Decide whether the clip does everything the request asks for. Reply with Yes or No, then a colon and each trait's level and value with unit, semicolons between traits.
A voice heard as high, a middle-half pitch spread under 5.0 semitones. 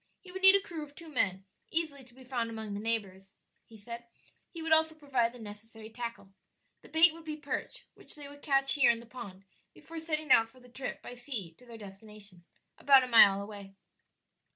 No: high, 245 Hz; wide, 5.6 semitones